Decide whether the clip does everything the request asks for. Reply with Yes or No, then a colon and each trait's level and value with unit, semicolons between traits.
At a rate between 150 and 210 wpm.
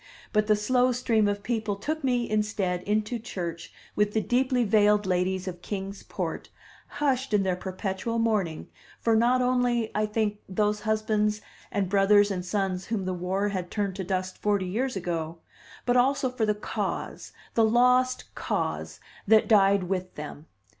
Yes: average, 165 wpm